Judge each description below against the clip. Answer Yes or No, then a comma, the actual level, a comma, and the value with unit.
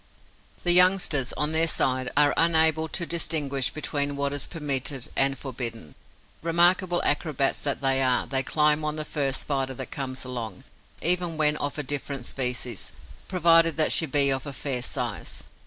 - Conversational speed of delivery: Yes, average, 165 wpm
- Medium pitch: Yes, medium, 145 Hz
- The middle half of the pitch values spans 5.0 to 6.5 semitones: No, average, 3.2 semitones